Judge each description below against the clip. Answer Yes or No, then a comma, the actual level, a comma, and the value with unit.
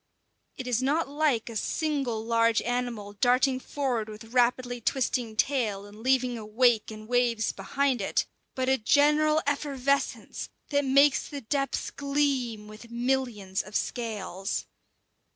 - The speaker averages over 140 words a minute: No, slow, 135 wpm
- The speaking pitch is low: No, high, 245 Hz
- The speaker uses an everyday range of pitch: Yes, average, 3.8 semitones